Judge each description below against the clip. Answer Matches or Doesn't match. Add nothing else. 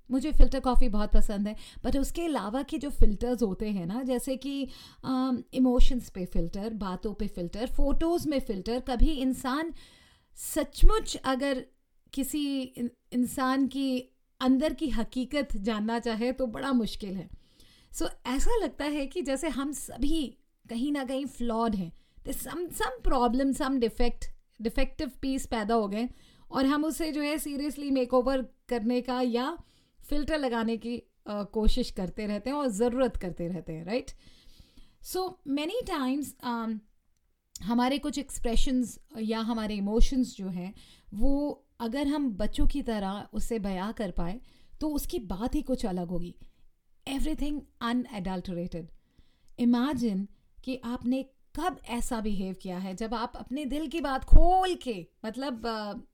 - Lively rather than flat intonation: Doesn't match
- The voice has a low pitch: Doesn't match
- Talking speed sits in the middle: Matches